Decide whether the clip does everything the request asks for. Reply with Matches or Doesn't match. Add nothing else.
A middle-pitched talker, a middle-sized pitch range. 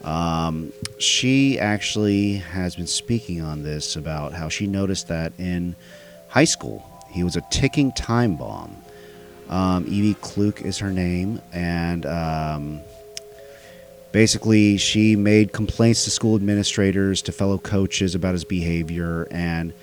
Doesn't match